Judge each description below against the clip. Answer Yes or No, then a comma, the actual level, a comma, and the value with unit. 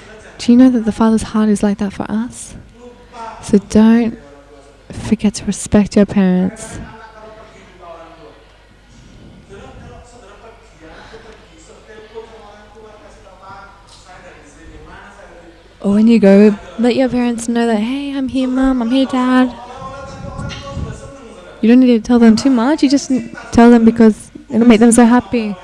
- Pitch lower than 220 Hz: No, high, 225 Hz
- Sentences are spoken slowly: Yes, slow, 125 wpm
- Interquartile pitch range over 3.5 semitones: No, average, 2.7 semitones